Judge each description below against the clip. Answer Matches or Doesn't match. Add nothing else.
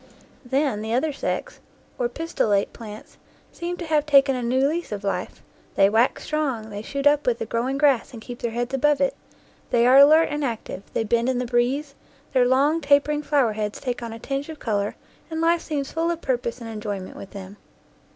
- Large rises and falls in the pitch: Doesn't match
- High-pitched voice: Matches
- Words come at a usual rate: Doesn't match